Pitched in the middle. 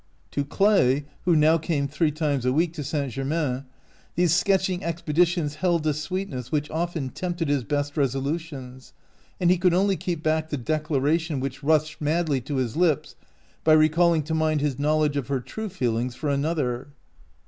Yes: medium, 155 Hz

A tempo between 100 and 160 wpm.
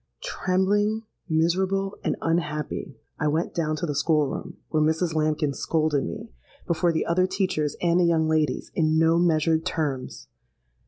Yes: average, 155 wpm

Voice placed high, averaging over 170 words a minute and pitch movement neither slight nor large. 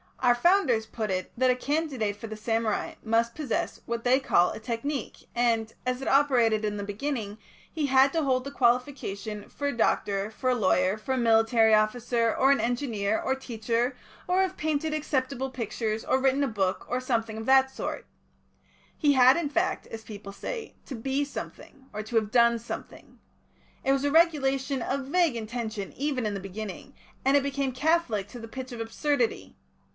Yes: high, 245 Hz; average, 190 wpm; average, 3.8 semitones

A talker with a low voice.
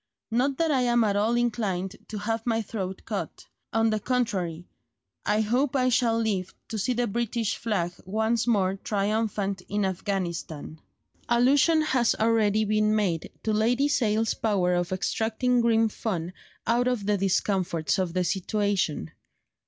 No: high, 215 Hz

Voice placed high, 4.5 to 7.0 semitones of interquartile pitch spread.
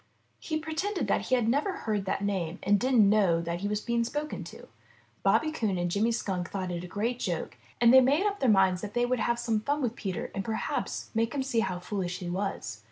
Yes: high, 215 Hz; average, 5.0 semitones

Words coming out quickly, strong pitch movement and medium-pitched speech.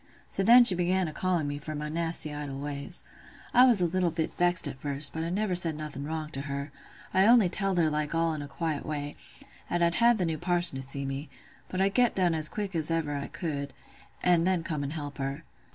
No: fast, 240 wpm; average, 3.8 semitones; medium, 160 Hz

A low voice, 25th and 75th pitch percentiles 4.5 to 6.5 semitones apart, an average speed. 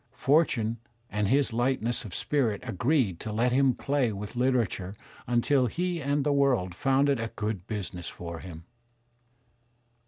Yes: low, 120 Hz; average, 4.9 semitones; average, 155 wpm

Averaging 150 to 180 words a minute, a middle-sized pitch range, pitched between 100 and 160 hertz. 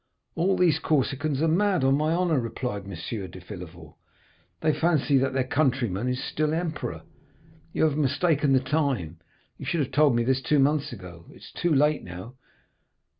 Yes: average, 175 wpm; average, 4.8 semitones; low, 135 Hz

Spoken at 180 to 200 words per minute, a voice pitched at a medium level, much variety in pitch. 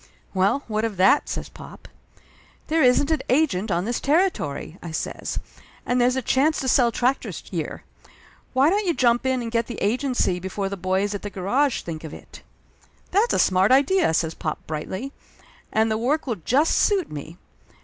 No: average, 185 wpm; high, 235 Hz; wide, 6.6 semitones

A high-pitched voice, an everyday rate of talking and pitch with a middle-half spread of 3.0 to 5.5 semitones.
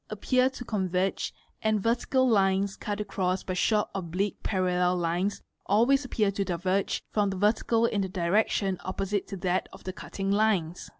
No: high, 195 Hz; average, 170 wpm; narrow, 2.6 semitones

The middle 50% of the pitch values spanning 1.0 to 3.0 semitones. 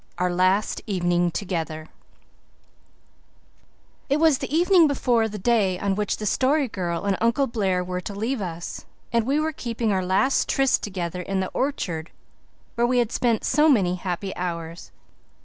No: wide, 5.6 semitones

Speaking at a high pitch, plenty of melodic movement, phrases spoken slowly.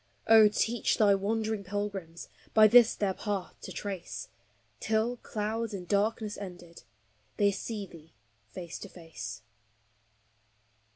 No: high, 205 Hz; average, 3.1 semitones; slow, 120 wpm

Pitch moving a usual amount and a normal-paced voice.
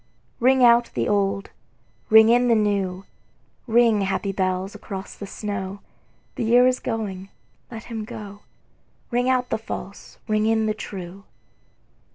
Yes: average, 3.1 semitones; average, 145 wpm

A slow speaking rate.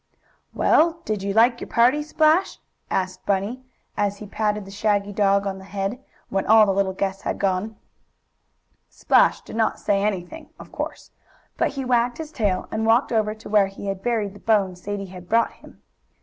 No: average, 190 wpm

